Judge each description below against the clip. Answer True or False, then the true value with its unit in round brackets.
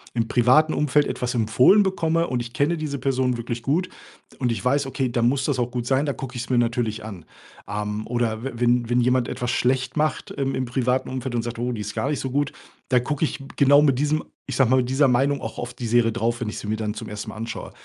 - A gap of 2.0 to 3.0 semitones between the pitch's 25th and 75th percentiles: True (2.7 semitones)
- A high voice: False (125 Hz)